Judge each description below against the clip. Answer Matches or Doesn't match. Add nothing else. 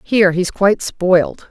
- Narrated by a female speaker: Matches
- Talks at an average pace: Matches